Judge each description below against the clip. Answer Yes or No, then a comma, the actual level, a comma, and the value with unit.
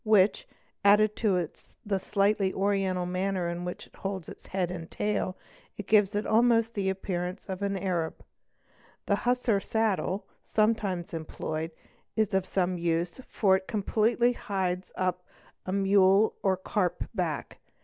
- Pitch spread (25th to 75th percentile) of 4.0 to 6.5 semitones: No, narrow, 2.5 semitones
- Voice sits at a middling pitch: No, high, 195 Hz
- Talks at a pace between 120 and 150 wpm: Yes, average, 140 wpm